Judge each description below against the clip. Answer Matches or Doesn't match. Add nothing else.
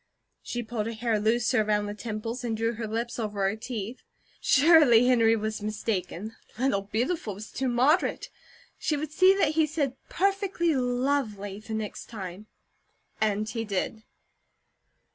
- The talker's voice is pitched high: Matches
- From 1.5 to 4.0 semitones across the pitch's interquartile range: Matches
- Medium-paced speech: Matches